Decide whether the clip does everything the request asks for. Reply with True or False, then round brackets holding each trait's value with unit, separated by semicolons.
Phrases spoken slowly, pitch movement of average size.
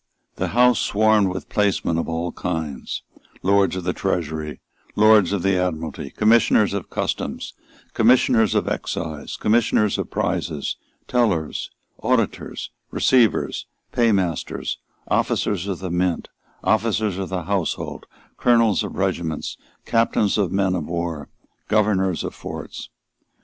True (125 wpm; 4.0 semitones)